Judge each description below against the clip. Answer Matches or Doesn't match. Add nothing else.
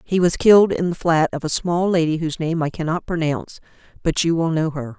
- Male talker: Doesn't match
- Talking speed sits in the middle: Doesn't match